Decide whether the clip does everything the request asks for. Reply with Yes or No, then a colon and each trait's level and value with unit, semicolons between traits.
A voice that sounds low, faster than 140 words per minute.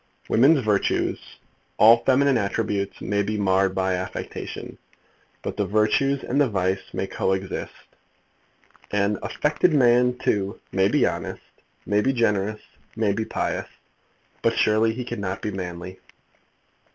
No: low, 105 Hz; slow, 135 wpm